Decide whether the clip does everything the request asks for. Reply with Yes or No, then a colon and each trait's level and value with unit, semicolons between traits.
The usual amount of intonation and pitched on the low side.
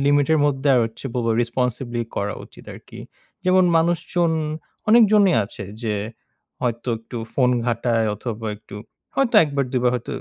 No: wide, 5.8 semitones; low, 125 Hz